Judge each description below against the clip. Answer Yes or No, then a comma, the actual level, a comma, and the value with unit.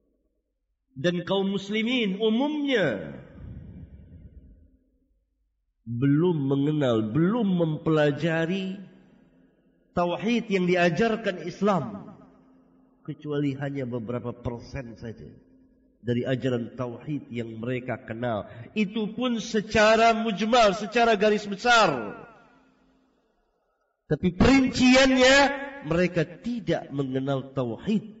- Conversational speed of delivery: No, slow, 75 wpm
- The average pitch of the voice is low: No, medium, 170 Hz